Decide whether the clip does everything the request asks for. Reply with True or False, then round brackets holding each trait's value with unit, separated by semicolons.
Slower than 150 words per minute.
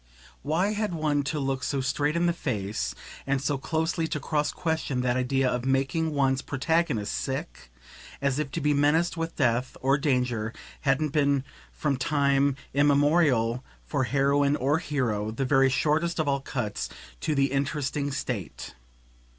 False (160 wpm)